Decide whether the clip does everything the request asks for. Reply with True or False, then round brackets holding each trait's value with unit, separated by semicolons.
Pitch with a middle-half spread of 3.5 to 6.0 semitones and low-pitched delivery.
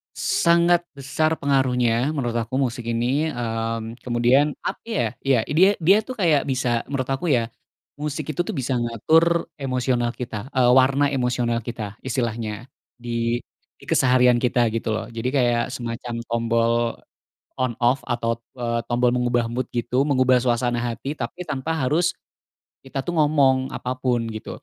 False (2.5 semitones; 125 Hz)